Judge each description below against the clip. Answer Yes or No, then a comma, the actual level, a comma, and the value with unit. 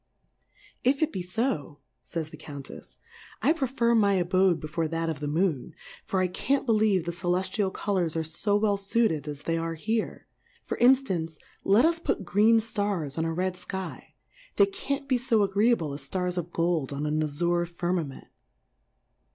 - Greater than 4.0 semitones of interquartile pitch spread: Yes, average, 5.0 semitones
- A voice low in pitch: No, medium, 180 Hz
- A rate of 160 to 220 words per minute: Yes, average, 170 wpm